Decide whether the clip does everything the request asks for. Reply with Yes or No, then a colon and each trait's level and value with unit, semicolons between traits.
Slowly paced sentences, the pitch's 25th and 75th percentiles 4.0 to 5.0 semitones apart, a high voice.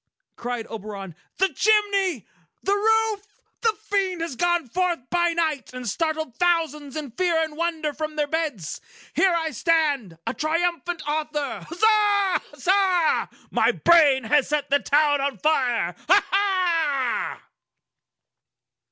Yes: slow, 125 wpm; average, 4.3 semitones; very high, 320 Hz